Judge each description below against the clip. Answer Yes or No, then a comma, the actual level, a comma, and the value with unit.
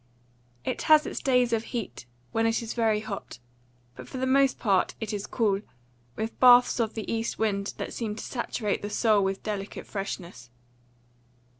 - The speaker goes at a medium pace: Yes, average, 175 wpm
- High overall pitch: Yes, high, 220 Hz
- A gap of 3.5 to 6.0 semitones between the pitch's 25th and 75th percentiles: No, average, 2.8 semitones